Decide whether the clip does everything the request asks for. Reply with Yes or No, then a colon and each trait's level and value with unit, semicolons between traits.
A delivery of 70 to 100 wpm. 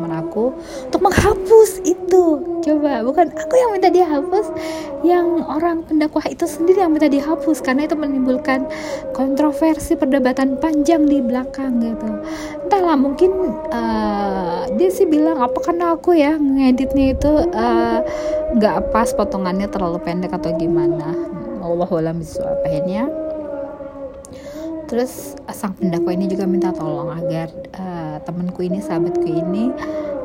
No: average, 125 wpm